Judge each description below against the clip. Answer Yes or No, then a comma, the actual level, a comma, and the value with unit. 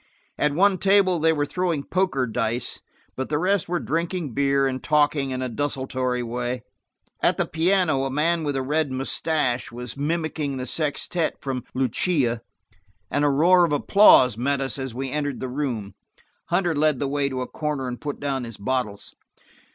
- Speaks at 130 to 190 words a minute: Yes, average, 180 wpm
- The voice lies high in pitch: No, medium, 140 Hz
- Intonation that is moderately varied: Yes, average, 3.8 semitones